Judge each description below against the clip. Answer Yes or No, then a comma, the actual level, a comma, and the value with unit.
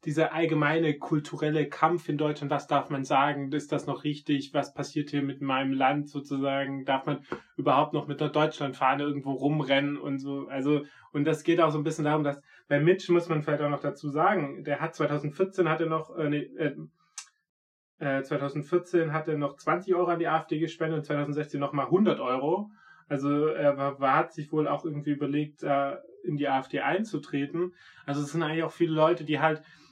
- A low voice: No, medium, 150 Hz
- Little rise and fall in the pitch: Yes, narrow, 2.0 semitones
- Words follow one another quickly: Yes, fast, 195 wpm